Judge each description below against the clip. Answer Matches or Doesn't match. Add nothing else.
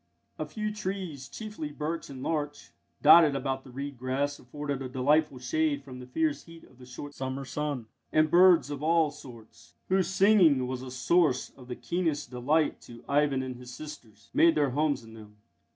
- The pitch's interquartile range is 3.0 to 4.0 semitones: Matches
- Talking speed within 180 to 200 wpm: Matches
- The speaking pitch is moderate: Matches